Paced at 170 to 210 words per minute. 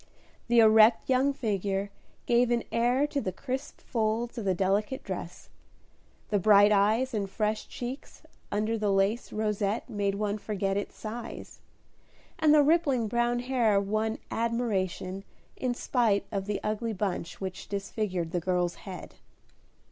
No: average, 145 wpm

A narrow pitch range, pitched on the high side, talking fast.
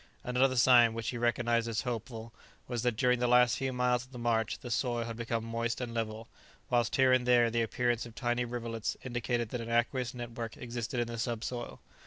No: narrow, 1.1 semitones; low, 120 Hz; fast, 210 wpm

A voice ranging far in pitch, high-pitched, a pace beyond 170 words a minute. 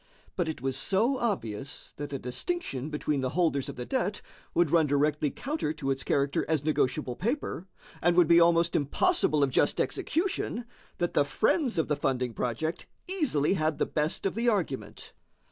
No: wide, 5.9 semitones; medium, 155 Hz; average, 180 wpm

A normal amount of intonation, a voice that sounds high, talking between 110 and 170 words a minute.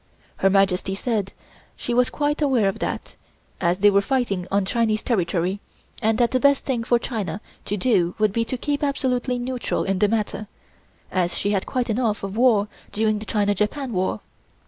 No: average, 4.1 semitones; high, 215 Hz; average, 190 wpm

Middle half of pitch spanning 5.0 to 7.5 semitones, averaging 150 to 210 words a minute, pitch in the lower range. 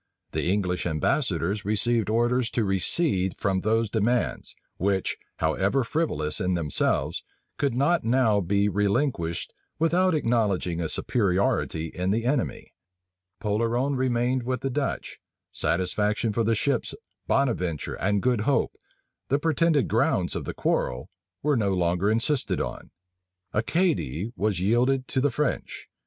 No: average, 5.3 semitones; slow, 135 wpm; low, 110 Hz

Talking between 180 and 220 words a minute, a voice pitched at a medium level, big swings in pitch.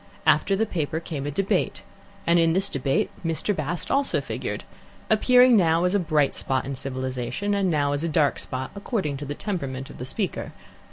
Yes: average, 185 wpm; medium, 160 Hz; wide, 6.0 semitones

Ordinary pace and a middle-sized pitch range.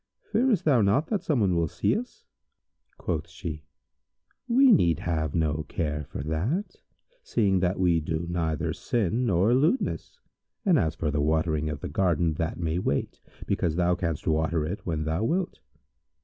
No: average, 165 wpm; wide, 6.4 semitones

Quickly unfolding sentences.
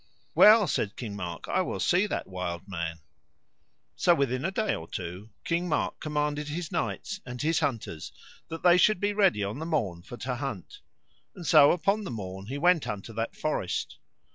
No: average, 190 wpm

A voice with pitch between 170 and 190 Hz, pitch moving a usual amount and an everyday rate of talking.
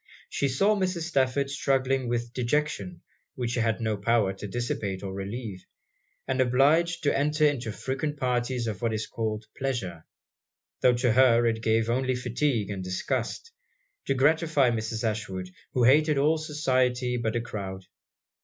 No: low, 125 Hz; average, 3.8 semitones; average, 155 wpm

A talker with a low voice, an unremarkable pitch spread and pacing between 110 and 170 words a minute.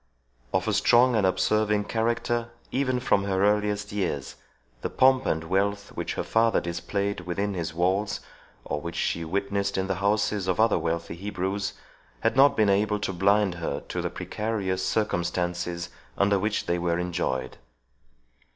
Yes: low, 100 Hz; average, 3.1 semitones; average, 160 wpm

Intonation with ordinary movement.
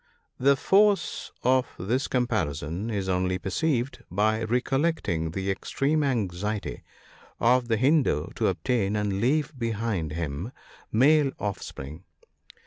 No: wide, 6.0 semitones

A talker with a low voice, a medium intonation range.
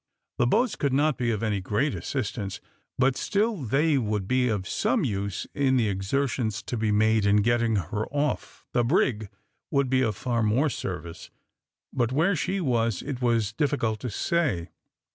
Yes: low, 120 Hz; average, 4.6 semitones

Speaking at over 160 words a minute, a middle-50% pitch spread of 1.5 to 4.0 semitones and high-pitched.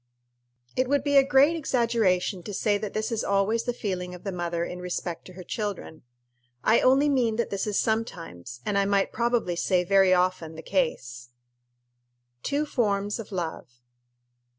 No: average, 175 wpm; average, 4.6 semitones; high, 200 Hz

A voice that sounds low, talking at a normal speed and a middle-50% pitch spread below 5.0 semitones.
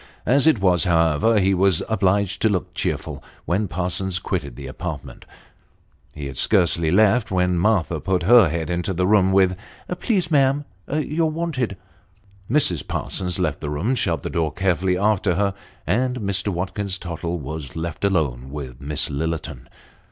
Yes: very low, 95 Hz; average, 160 wpm; average, 4.2 semitones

